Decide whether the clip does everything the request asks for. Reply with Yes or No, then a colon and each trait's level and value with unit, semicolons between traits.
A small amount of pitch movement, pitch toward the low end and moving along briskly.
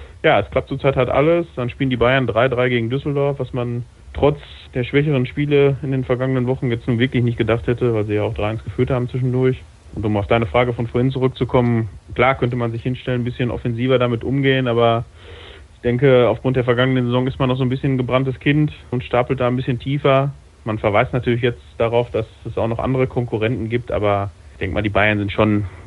Yes: narrow, 2.1 semitones; low, 125 Hz; fast, 225 wpm